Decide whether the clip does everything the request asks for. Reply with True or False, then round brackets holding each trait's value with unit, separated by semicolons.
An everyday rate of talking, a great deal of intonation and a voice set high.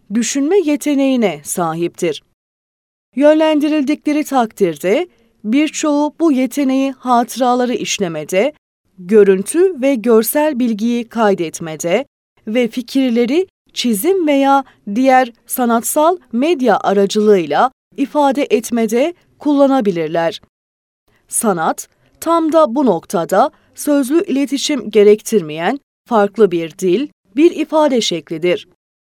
False (85 wpm; 6.5 semitones; 245 Hz)